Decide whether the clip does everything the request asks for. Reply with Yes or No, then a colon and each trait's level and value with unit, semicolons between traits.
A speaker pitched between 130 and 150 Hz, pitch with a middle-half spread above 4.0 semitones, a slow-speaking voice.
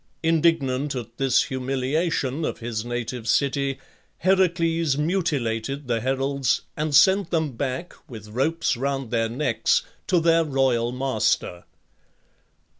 Yes: low, 135 Hz; average, 4.7 semitones; slow, 115 wpm